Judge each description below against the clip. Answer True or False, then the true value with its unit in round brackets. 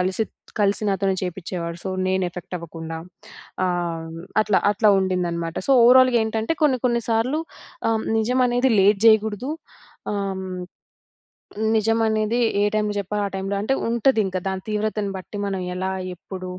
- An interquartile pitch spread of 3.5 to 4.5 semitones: False (3.1 semitones)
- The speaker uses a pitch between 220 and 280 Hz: False (205 Hz)